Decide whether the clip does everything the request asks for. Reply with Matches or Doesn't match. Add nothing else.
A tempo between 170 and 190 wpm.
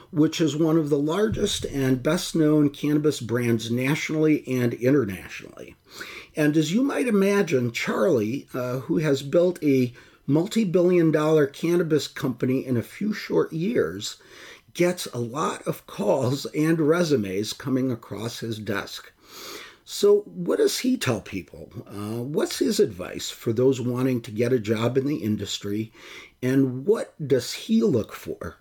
Doesn't match